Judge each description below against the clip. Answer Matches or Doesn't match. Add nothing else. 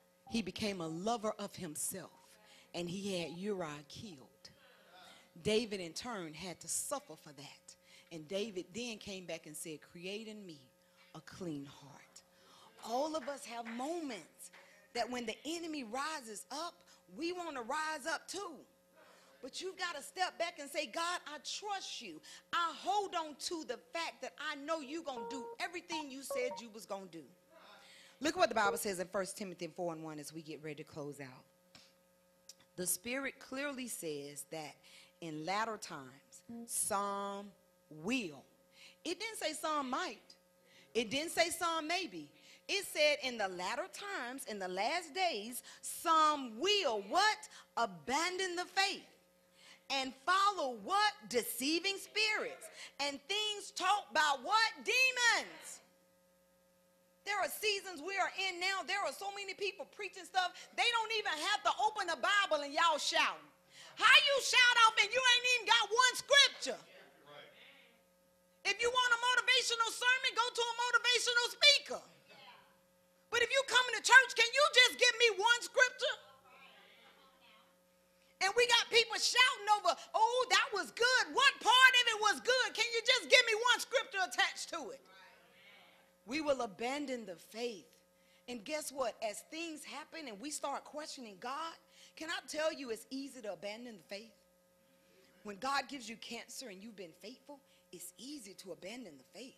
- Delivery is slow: Doesn't match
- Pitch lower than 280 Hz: Doesn't match